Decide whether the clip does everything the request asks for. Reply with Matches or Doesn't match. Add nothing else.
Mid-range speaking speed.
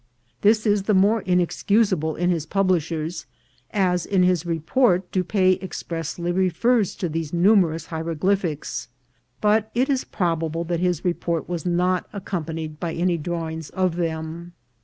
Matches